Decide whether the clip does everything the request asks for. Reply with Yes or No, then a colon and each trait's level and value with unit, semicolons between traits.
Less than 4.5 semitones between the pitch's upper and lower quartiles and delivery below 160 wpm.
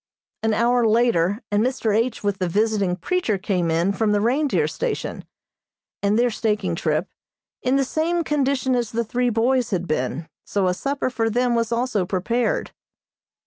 No: average, 4.0 semitones; average, 170 wpm